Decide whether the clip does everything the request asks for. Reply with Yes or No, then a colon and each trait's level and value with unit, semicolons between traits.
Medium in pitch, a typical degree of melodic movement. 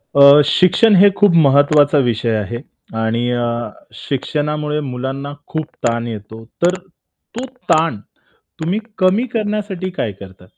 No: medium, 145 Hz; wide, 7.6 semitones